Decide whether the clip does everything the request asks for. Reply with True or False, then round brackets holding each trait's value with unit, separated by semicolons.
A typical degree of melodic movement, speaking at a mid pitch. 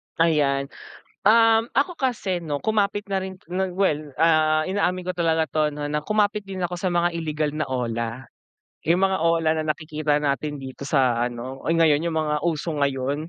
True (4.1 semitones; 160 Hz)